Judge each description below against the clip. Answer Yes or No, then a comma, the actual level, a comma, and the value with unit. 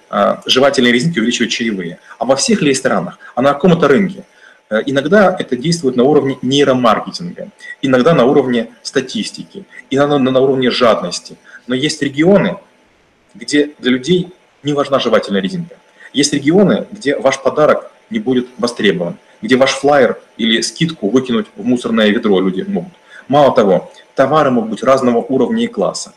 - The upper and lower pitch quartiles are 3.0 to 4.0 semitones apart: No, average, 4.6 semitones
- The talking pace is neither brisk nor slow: Yes, average, 145 wpm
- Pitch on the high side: No, low, 135 Hz